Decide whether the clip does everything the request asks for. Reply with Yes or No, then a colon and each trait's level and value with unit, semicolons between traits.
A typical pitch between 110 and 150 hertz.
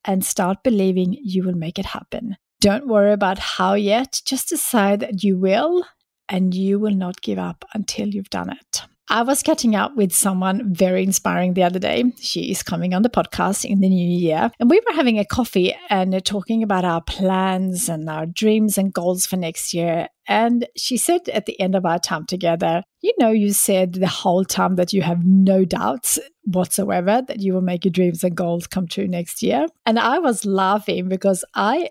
No: high, 195 Hz